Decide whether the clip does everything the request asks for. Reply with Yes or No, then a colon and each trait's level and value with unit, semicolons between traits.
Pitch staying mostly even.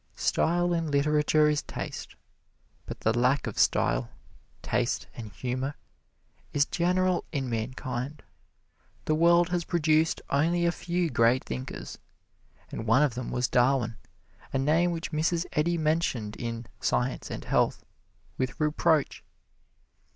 No: average, 5.2 semitones